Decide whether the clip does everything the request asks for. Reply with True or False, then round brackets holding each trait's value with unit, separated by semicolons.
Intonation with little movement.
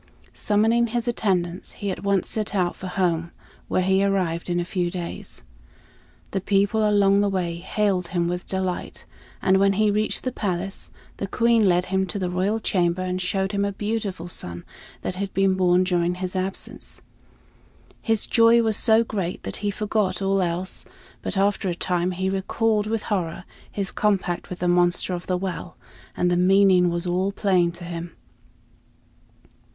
True (2.3 semitones)